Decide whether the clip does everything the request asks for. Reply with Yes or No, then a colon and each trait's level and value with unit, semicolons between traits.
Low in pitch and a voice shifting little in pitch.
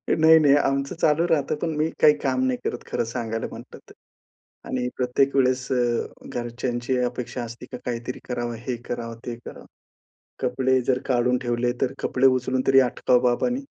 Yes: low, 125 Hz; narrow, 2.1 semitones